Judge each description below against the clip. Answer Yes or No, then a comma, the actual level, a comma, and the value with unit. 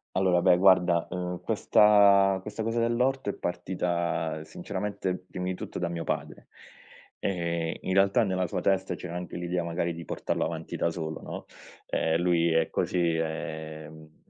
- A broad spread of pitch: No, narrow, 2.4 semitones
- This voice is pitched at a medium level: No, very low, 90 Hz